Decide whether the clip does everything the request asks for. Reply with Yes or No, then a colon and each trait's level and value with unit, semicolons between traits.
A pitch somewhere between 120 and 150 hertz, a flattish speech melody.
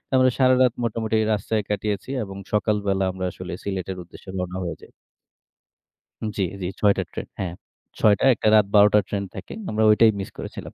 No: low, 105 Hz; narrow, 2.3 semitones